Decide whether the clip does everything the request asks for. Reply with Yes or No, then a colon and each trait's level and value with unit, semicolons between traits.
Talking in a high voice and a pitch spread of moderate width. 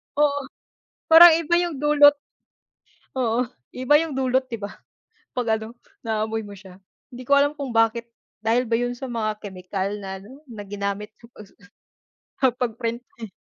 Yes: high, 235 Hz; average, 3.9 semitones